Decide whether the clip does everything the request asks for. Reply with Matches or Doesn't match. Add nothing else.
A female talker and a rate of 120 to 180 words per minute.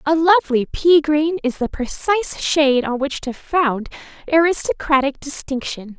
Matches